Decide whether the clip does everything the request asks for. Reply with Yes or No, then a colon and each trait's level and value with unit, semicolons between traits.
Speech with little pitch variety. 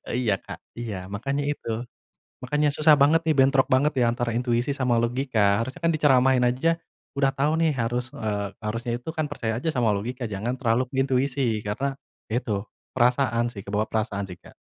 No: average, 3.2 semitones